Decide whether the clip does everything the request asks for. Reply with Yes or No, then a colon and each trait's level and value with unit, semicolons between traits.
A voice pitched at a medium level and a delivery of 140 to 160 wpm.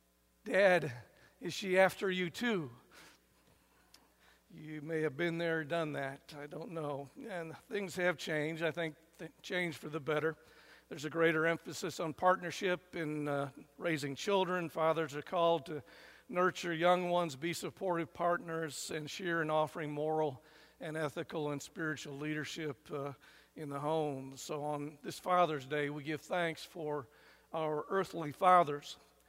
Yes: medium, 160 Hz; average, 150 wpm